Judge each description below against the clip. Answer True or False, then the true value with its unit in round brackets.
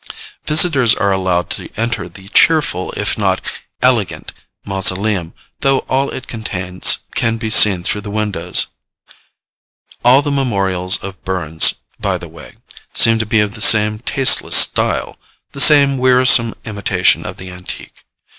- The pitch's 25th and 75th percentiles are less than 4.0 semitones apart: False (5.2 semitones)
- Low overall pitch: True (105 Hz)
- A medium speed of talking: True (145 wpm)